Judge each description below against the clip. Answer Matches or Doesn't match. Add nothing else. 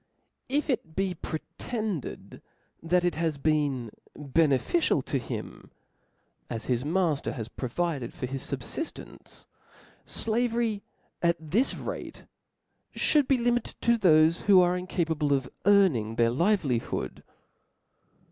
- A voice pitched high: Doesn't match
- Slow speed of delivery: Matches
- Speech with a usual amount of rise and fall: Doesn't match